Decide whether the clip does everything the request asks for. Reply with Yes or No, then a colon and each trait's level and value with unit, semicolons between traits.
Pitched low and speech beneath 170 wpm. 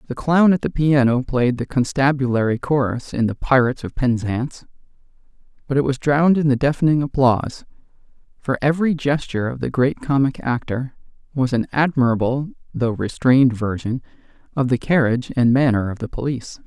Yes: low, 130 Hz; average, 160 wpm